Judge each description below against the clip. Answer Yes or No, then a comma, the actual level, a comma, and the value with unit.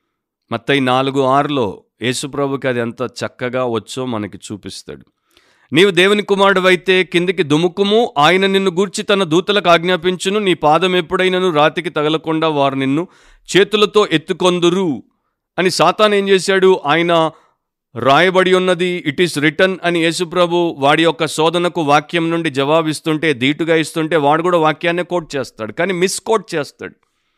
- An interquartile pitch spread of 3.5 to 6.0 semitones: Yes, average, 4.0 semitones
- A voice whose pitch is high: No, medium, 170 Hz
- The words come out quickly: Yes, fast, 130 wpm